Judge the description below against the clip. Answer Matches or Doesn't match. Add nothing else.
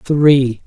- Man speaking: Matches